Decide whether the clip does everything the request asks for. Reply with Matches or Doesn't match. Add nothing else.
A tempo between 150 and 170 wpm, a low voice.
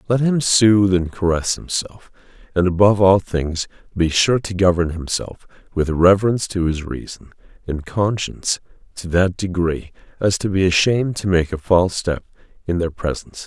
Matches